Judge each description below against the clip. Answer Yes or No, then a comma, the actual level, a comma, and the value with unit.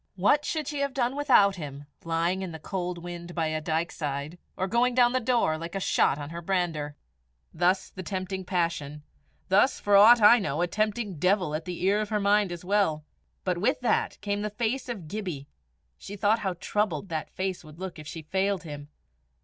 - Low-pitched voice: No, medium, 185 Hz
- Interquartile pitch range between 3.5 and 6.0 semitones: Yes, average, 4.1 semitones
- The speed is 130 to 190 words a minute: No, fast, 205 wpm